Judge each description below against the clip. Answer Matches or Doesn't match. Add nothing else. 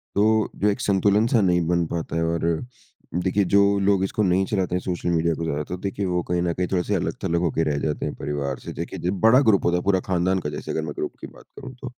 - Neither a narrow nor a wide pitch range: Matches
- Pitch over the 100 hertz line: Doesn't match